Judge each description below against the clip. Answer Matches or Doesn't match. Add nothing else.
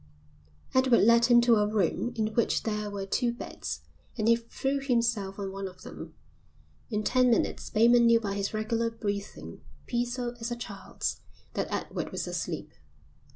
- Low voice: Doesn't match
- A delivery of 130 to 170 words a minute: Matches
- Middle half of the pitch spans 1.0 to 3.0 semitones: Matches